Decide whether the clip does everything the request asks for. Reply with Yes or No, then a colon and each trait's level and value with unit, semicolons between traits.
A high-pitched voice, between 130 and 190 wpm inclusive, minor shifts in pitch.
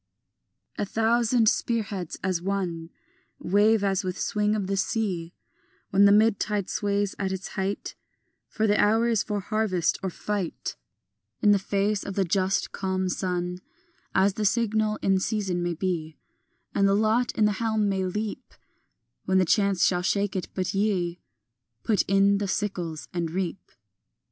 Yes: high, 200 Hz; average, 160 wpm; narrow, 2.2 semitones